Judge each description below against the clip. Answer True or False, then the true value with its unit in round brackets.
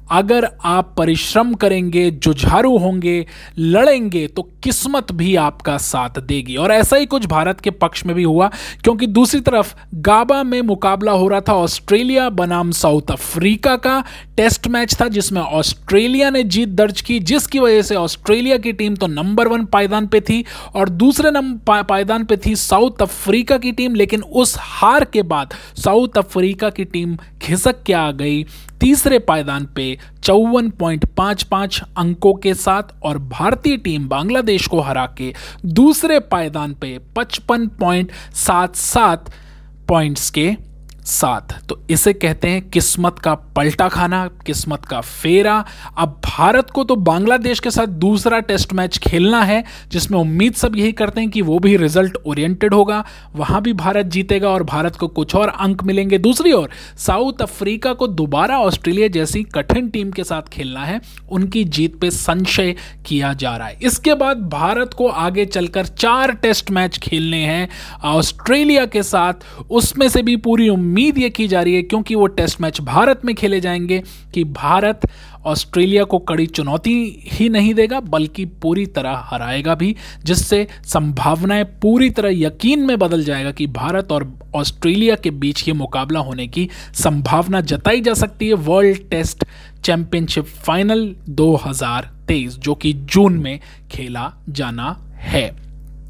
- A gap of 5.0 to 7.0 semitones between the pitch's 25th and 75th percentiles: True (5.5 semitones)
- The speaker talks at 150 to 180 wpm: True (160 wpm)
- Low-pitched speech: False (190 Hz)